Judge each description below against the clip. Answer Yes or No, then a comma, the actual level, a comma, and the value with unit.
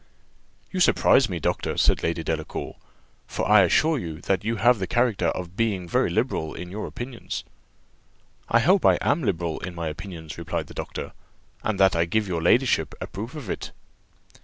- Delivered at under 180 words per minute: No, average, 185 wpm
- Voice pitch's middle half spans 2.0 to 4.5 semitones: No, wide, 5.6 semitones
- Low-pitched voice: Yes, very low, 95 Hz